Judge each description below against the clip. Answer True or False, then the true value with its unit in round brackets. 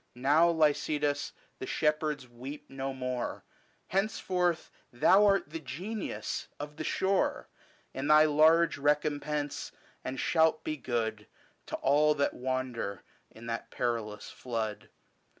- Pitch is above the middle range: False (145 Hz)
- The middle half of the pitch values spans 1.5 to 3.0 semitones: False (3.6 semitones)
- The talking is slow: True (125 wpm)